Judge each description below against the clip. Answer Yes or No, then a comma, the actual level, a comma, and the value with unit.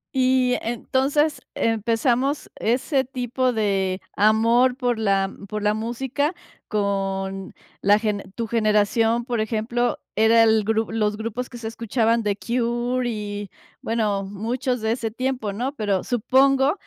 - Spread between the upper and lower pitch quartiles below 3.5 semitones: Yes, average, 2.9 semitones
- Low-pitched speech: No, high, 230 Hz